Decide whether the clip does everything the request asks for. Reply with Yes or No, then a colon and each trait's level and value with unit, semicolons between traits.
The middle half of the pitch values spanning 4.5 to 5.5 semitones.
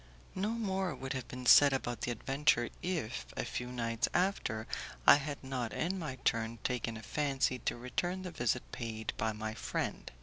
Yes: average, 5.0 semitones